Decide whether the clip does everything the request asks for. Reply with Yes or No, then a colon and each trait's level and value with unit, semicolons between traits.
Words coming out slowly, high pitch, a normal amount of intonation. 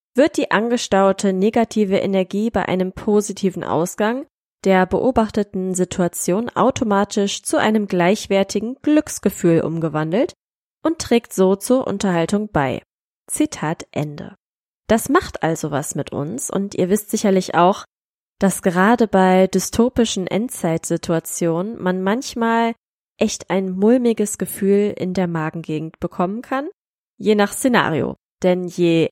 Yes: slow, 120 wpm; high, 195 Hz; average, 4.0 semitones